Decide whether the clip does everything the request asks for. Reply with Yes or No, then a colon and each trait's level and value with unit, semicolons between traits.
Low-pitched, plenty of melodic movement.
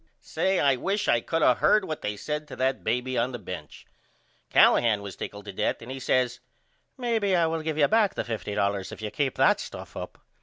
Yes: low, 130 Hz; wide, 7.2 semitones